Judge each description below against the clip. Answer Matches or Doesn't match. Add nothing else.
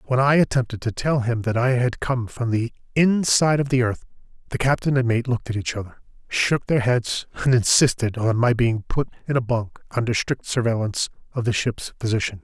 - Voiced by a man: Matches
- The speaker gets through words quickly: Matches